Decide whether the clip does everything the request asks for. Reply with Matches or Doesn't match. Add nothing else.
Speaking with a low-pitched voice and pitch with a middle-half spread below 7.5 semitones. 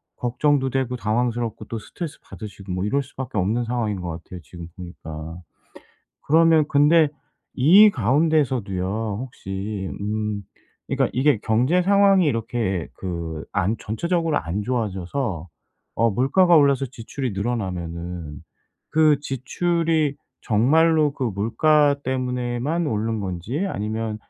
Matches